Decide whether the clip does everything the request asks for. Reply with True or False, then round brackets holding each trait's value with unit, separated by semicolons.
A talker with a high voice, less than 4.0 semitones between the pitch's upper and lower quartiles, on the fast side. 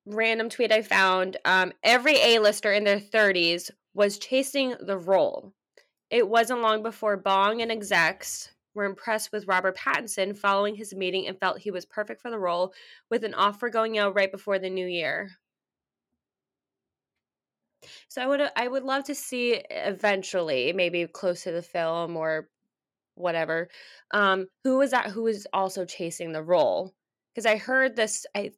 False (205 Hz; 3.5 semitones; 165 wpm)